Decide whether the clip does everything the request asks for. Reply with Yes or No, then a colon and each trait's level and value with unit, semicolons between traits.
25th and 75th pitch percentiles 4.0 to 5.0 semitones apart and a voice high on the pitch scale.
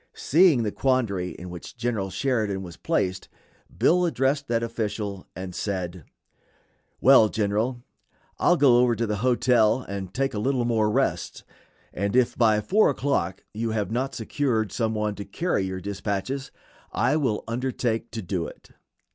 No: average, 4.3 semitones; low, 110 Hz